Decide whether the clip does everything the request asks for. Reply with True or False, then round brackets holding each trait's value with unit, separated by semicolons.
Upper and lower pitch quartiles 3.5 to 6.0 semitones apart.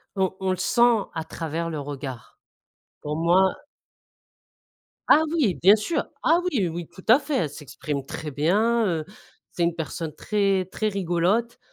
True (4.9 semitones)